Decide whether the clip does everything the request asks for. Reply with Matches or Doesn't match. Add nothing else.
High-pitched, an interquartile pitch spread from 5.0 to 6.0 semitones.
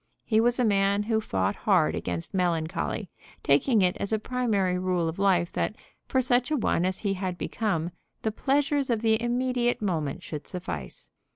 Matches